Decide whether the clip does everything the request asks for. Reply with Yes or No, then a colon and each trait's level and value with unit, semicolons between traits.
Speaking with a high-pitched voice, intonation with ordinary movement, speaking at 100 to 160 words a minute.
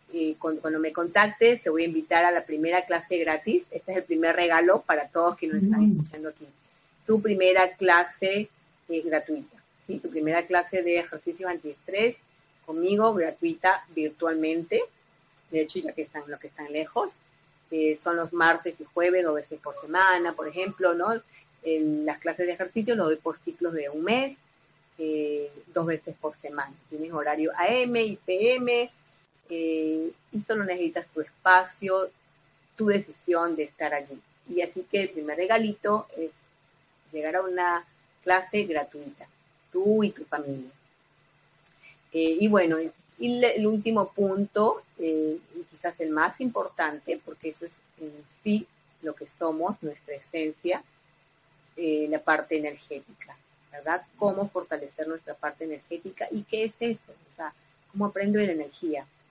No: medium, 165 Hz; average, 3.3 semitones; average, 155 wpm